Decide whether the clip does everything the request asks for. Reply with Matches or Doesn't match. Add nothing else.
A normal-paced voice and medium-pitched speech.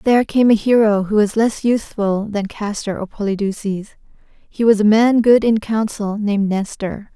Doesn't match